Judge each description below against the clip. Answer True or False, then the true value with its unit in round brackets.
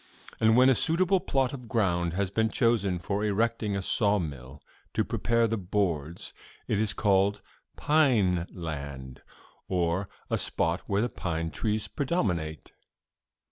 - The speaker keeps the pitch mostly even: False (5.0 semitones)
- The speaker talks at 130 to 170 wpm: True (140 wpm)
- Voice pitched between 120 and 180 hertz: False (100 Hz)